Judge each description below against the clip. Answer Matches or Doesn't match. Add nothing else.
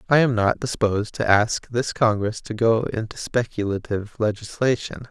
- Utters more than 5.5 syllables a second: Doesn't match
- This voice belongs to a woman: Doesn't match